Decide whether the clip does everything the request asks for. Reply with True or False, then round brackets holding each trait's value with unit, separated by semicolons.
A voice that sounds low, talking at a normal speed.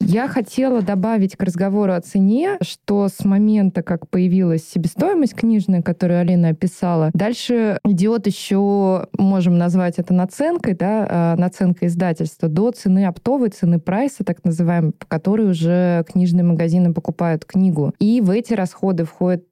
False (185 Hz; 140 wpm)